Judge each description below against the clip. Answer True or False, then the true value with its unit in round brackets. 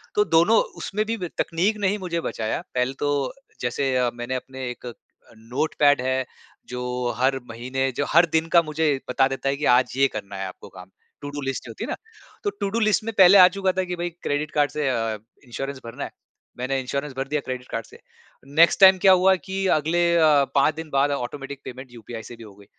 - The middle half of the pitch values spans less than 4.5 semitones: False (5.1 semitones)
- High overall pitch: False (140 Hz)